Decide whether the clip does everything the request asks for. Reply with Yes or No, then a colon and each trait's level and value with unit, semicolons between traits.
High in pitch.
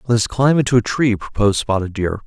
No: low, 115 Hz